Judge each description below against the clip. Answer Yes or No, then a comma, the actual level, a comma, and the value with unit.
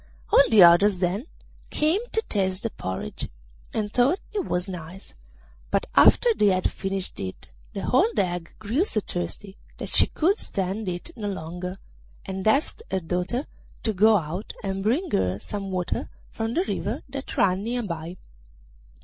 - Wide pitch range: No, average, 4.5 semitones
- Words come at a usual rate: Yes, average, 160 wpm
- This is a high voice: Yes, high, 195 Hz